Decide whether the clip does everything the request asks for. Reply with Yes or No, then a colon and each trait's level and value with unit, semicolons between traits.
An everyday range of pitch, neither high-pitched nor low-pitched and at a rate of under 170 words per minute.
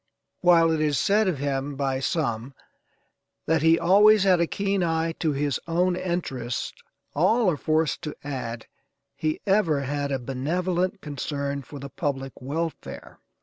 Yes: average, 4.2 semitones; medium, 155 Hz; average, 150 wpm